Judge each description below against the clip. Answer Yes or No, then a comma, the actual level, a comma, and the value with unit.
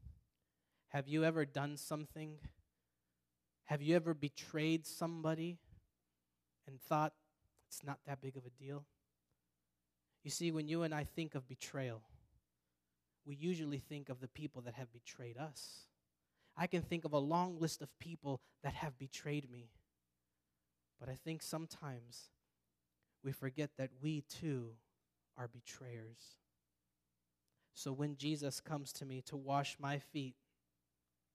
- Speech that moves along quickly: No, average, 140 wpm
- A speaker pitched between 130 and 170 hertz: Yes, low, 135 Hz